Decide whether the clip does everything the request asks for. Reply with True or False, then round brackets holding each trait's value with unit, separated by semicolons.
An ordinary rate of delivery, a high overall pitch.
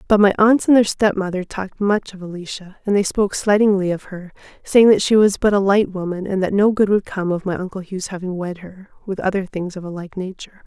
False (250 wpm; 195 Hz)